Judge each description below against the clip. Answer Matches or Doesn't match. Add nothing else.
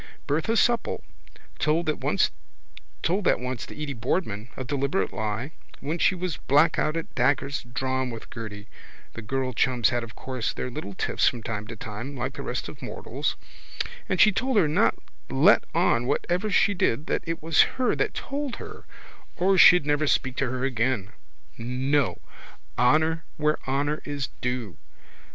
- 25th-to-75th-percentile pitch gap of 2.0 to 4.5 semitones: Doesn't match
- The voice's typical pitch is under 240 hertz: Matches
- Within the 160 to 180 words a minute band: Matches